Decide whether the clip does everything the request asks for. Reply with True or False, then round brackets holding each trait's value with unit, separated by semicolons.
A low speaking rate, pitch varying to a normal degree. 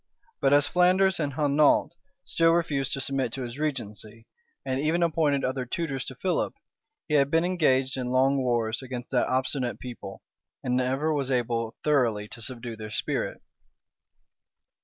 False (160 wpm; 3.4 semitones)